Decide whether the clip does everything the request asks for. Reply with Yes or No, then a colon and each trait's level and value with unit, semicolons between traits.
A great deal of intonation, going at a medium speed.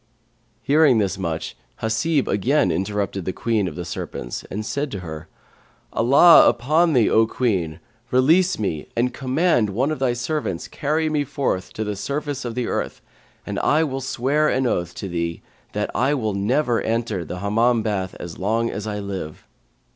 Yes: wide, 6.1 semitones; average, 175 wpm